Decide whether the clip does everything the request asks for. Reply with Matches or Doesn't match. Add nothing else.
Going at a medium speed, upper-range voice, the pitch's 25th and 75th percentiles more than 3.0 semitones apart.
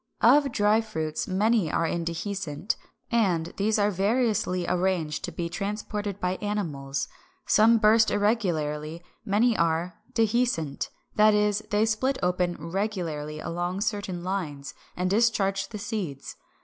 Doesn't match